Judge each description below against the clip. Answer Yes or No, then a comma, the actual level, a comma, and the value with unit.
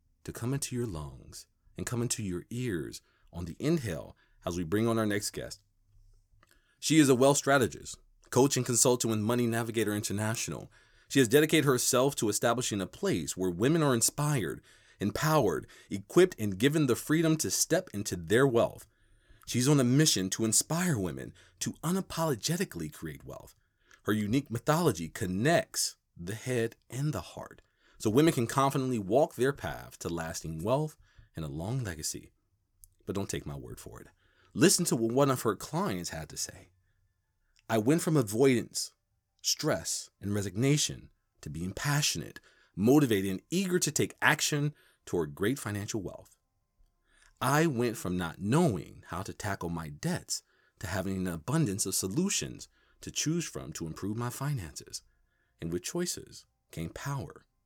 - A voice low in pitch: Yes, low, 115 Hz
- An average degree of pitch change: No, wide, 6.9 semitones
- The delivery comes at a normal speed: Yes, average, 160 wpm